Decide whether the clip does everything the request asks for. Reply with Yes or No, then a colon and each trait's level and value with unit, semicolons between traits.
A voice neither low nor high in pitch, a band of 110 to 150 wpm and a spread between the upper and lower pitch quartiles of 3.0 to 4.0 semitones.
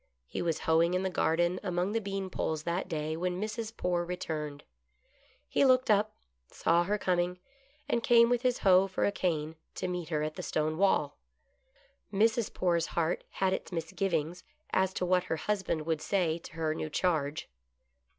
No: medium, 180 Hz; average, 180 wpm; average, 3.3 semitones